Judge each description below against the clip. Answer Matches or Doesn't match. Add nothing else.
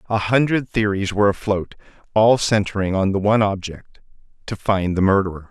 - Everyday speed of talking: Matches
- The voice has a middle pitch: Doesn't match